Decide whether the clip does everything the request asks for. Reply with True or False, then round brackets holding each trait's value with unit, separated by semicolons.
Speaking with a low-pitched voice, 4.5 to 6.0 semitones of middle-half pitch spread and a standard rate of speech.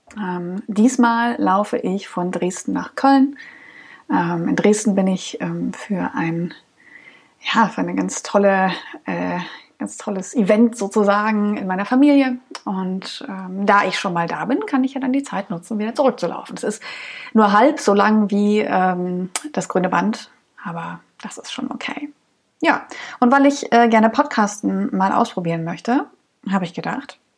False (210 Hz; 5.2 semitones; 165 wpm)